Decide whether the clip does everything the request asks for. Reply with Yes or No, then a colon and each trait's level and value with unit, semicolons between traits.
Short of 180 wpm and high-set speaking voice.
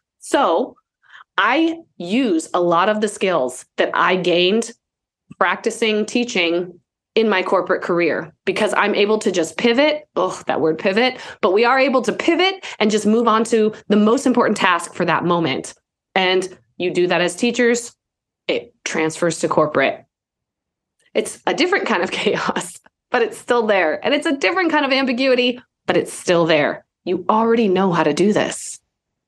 Yes: average, 170 wpm; high, 210 Hz